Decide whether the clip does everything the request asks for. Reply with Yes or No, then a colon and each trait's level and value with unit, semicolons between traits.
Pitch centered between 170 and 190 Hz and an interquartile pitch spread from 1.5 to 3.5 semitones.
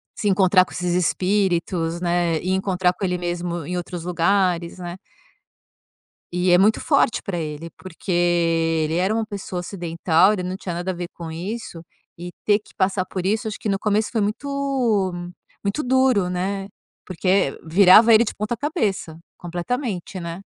Yes: medium, 185 Hz; average, 2.8 semitones